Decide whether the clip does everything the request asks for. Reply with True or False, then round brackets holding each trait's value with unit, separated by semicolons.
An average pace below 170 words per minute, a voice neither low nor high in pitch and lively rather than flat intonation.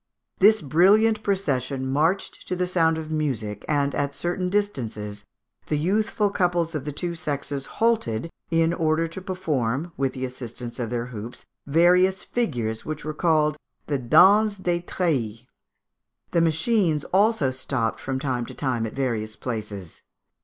True (150 wpm; 150 Hz; 6.0 semitones)